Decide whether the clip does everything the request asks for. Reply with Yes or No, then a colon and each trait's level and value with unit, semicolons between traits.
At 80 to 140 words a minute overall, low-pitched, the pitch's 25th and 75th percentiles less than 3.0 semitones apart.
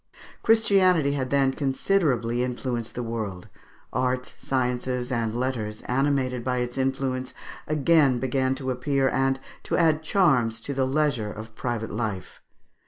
Yes: slow, 135 wpm; low, 130 Hz; narrow, 2.4 semitones